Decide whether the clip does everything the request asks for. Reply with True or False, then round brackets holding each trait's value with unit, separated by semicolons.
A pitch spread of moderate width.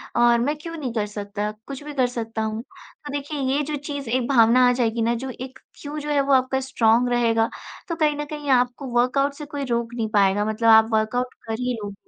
True (3.8 semitones)